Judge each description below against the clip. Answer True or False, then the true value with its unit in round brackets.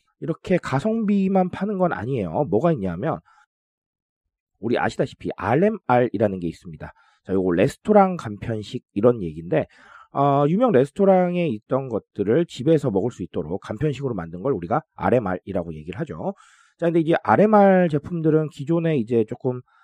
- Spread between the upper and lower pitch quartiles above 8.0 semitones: True (8.5 semitones)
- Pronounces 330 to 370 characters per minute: True (350 characters per minute)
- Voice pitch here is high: False (145 Hz)